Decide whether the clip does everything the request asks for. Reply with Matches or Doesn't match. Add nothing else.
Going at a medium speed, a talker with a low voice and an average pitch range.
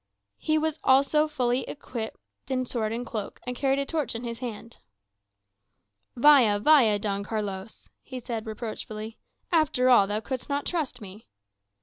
Doesn't match